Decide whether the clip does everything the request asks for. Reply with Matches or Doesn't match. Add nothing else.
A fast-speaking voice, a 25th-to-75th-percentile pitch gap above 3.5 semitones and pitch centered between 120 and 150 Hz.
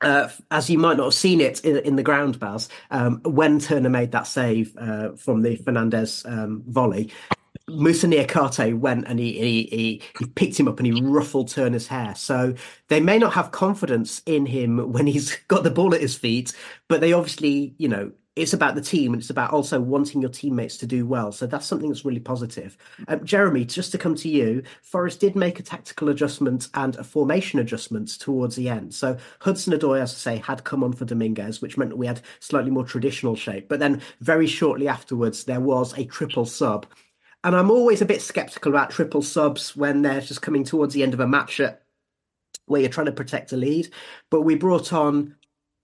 Matches